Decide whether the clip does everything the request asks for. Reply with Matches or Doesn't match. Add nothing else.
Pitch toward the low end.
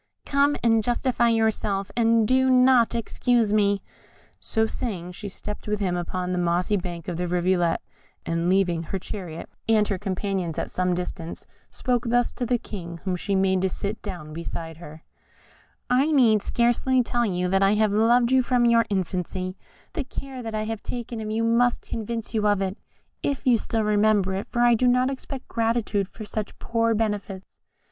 Doesn't match